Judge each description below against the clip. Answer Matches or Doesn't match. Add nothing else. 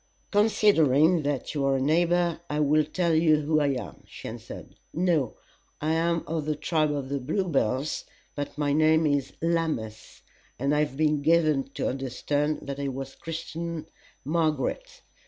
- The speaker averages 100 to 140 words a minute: Doesn't match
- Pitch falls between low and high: Matches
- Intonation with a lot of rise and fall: Doesn't match